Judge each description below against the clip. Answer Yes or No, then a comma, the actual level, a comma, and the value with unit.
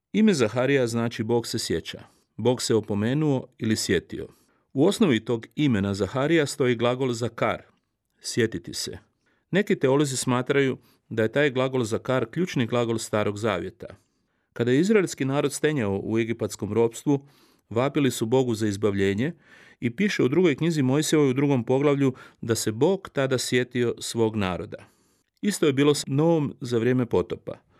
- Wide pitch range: No, average, 3.9 semitones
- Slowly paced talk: No, average, 155 wpm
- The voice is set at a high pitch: No, low, 125 Hz